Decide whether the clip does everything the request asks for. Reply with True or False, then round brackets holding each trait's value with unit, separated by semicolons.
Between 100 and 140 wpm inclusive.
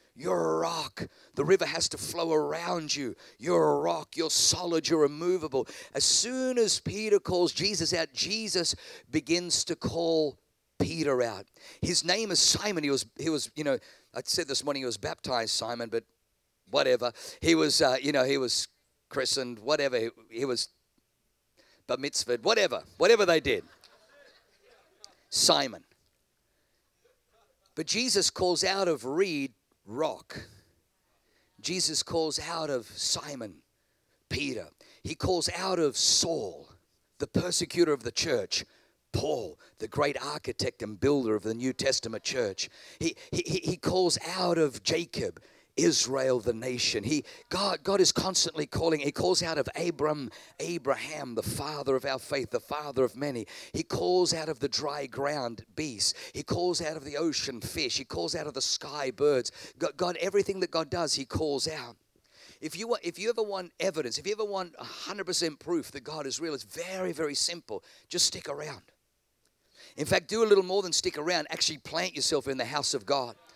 False (170 wpm)